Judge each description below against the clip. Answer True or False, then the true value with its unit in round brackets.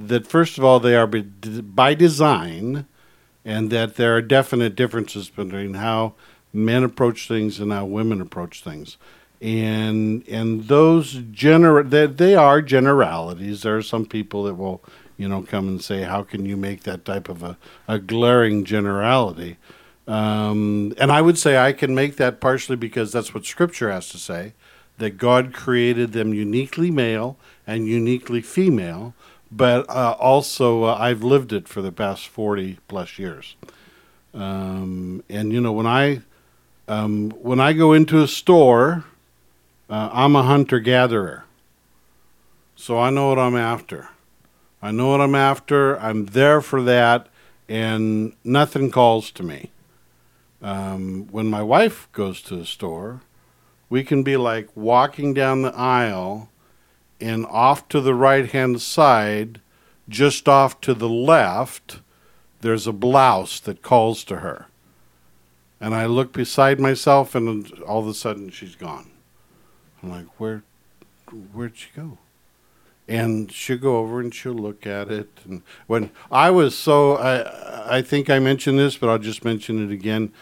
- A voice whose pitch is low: True (115 Hz)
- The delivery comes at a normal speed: True (155 wpm)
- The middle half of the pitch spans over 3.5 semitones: True (4.0 semitones)